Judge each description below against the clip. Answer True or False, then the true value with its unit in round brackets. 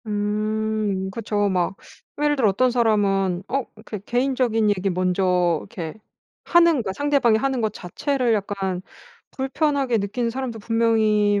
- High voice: True (215 Hz)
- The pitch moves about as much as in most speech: True (4.1 semitones)